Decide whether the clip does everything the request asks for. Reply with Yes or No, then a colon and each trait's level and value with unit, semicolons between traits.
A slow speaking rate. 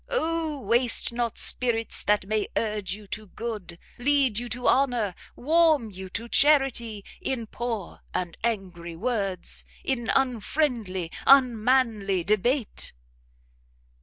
Yes: slow, 115 wpm